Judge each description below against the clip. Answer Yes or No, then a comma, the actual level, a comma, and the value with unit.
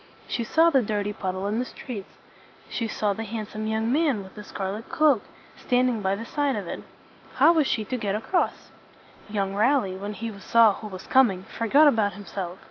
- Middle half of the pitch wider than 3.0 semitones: Yes, average, 3.8 semitones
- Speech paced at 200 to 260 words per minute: Yes, fast, 205 wpm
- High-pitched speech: Yes, high, 215 Hz